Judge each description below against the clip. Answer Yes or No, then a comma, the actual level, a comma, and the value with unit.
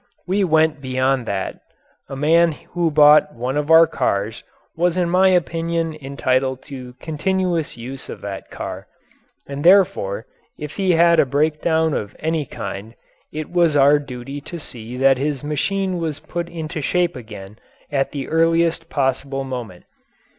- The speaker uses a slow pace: No, average, 155 wpm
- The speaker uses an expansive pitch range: No, average, 4.2 semitones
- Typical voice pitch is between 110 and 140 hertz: No, medium, 150 Hz